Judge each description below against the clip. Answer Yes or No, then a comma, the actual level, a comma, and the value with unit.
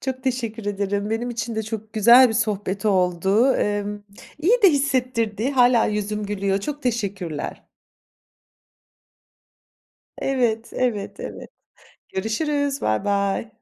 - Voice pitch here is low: No, high, 220 Hz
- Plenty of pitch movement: No, average, 3.8 semitones